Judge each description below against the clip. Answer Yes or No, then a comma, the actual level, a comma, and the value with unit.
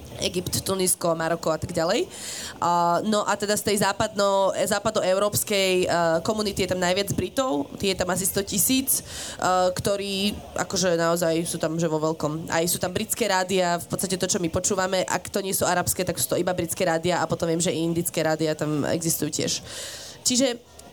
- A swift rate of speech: Yes, fast, 190 wpm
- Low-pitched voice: No, medium, 185 Hz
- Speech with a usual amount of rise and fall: Yes, average, 3.0 semitones